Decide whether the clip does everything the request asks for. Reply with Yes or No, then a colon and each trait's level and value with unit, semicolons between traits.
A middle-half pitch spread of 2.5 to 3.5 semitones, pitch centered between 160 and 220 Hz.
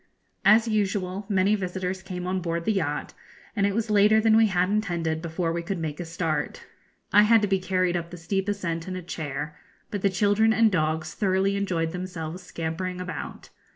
Yes: average, 3.2 semitones; medium, 185 Hz